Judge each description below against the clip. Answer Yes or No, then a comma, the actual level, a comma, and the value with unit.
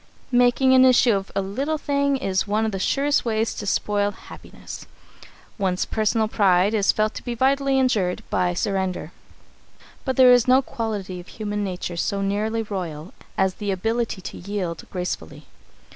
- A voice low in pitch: No, high, 210 Hz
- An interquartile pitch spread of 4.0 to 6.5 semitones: Yes, average, 4.4 semitones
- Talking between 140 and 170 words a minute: Yes, average, 165 wpm